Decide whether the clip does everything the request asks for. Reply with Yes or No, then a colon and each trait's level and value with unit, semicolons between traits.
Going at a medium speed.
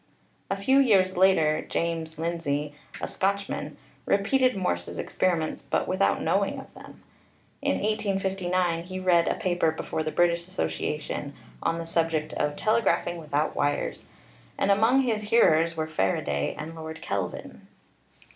Yes: average, 145 wpm